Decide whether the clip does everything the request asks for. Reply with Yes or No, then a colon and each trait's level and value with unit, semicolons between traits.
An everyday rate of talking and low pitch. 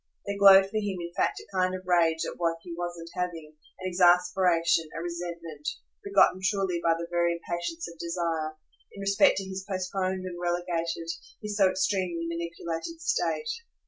No: average, 170 wpm; medium, 175 Hz